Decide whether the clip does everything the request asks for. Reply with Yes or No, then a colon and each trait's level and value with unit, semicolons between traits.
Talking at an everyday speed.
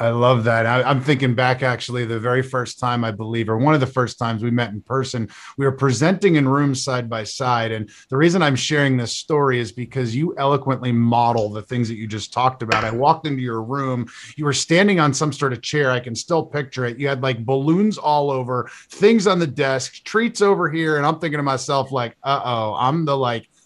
No: fast, 235 wpm